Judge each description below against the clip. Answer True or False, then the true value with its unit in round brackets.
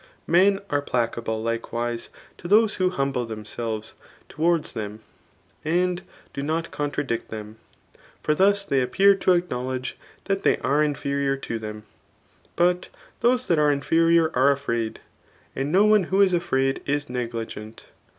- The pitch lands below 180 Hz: True (140 Hz)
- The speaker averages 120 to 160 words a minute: True (145 wpm)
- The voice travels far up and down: True (6.9 semitones)